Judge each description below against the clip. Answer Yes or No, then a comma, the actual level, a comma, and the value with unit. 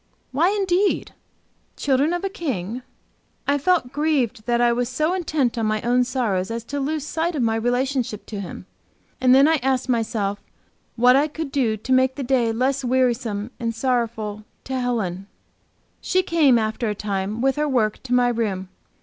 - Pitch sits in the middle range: No, very high, 250 Hz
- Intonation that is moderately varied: Yes, average, 3.9 semitones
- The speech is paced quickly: No, average, 180 wpm